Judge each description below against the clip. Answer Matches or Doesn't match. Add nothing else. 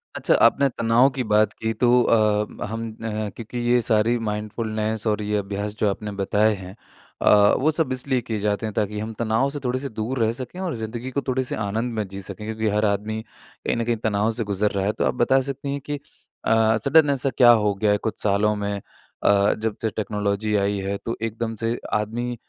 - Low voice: Matches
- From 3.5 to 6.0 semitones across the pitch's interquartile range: Doesn't match